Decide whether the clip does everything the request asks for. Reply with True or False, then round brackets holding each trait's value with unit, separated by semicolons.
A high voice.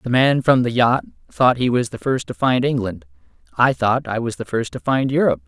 False (125 Hz)